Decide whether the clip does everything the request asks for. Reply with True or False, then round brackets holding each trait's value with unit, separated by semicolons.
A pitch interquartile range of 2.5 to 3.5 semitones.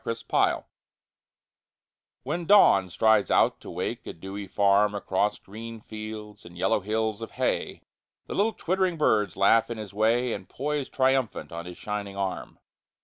True (2.9 semitones)